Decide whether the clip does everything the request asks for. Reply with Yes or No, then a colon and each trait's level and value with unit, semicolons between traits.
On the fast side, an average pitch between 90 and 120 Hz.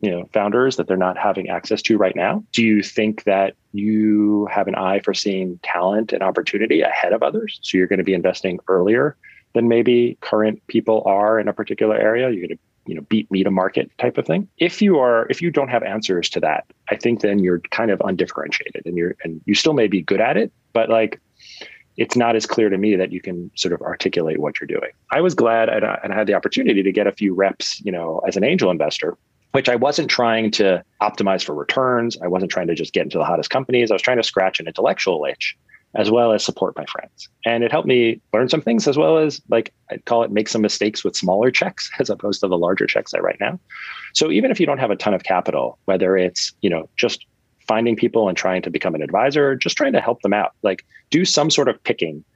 Yes: fast, 245 wpm; low, 110 Hz